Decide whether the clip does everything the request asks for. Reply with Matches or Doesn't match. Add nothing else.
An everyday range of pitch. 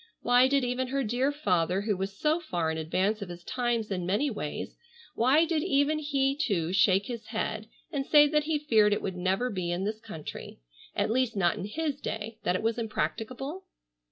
Doesn't match